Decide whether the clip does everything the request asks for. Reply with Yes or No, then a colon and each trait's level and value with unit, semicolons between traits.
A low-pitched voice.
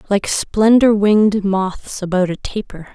No: high, 200 Hz